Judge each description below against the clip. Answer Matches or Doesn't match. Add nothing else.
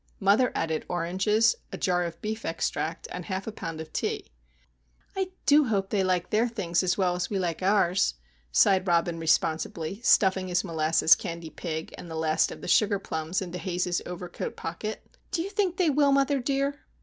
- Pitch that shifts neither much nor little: Matches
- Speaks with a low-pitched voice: Doesn't match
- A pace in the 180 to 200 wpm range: Matches